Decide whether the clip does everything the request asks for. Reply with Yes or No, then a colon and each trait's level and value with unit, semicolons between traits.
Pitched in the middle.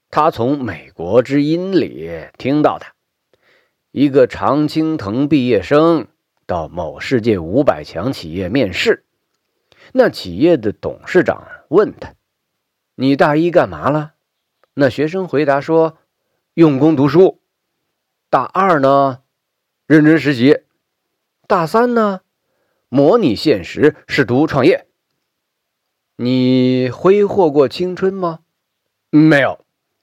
Yes: medium, 155 Hz